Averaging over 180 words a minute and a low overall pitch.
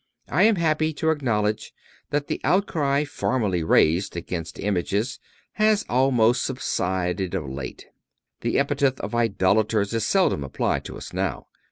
No: average, 140 wpm; low, 115 Hz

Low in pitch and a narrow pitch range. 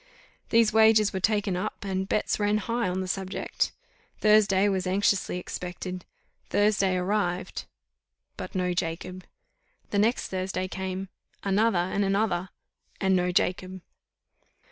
No: high, 190 Hz; narrow, 2.0 semitones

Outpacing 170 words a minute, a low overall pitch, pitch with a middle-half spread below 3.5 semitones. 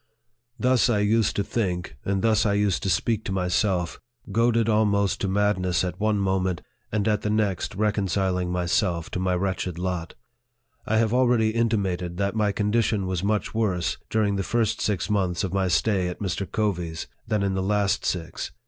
Yes: average, 180 wpm; low, 100 Hz; average, 2.8 semitones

